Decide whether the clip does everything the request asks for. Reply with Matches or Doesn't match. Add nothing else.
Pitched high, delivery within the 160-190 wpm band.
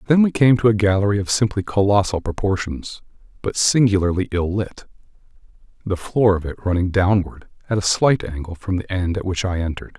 Doesn't match